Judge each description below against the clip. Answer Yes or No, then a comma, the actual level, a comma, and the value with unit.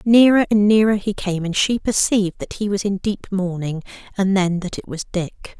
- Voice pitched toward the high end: Yes, high, 195 Hz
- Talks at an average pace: No, fast, 215 wpm